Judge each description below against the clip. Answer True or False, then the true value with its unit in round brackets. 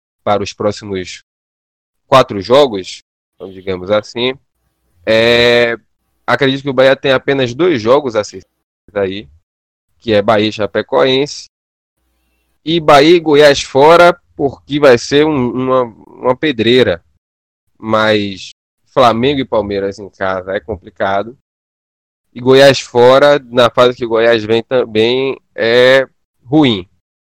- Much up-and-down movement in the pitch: True (6.4 semitones)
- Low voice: True (110 Hz)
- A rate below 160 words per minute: True (120 wpm)